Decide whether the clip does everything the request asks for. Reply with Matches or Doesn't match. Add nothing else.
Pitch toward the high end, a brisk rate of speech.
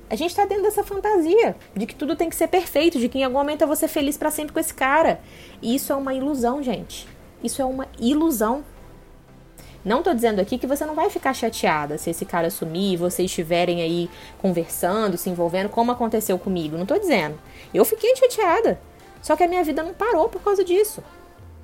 Matches